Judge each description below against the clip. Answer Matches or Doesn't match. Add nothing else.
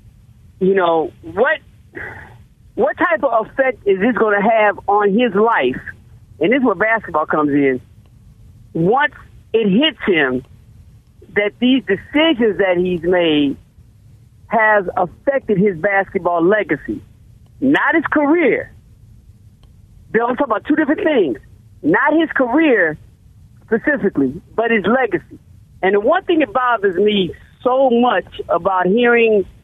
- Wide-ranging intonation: Matches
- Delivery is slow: Matches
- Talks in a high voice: Matches